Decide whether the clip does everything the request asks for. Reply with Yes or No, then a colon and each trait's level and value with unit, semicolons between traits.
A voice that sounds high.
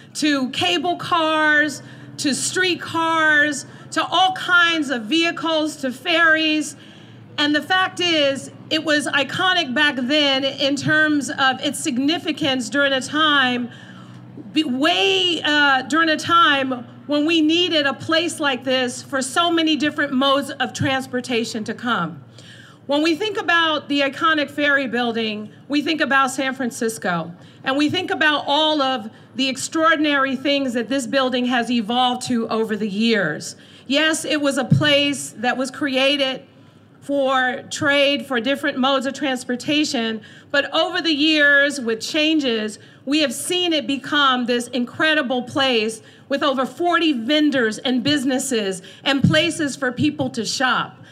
Yes: very high, 280 Hz